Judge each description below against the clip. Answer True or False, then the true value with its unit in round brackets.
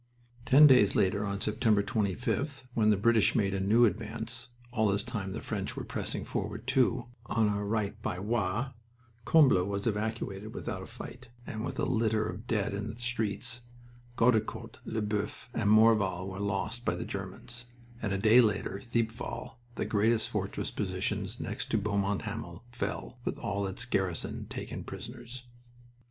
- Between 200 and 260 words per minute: False (165 wpm)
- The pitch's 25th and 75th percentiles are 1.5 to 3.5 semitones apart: True (2.7 semitones)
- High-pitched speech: False (110 Hz)